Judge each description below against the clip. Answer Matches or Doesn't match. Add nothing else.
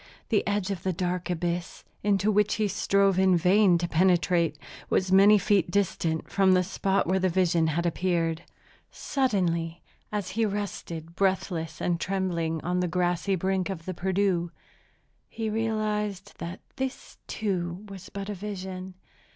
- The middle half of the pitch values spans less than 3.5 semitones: Matches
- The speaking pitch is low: Doesn't match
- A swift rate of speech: Doesn't match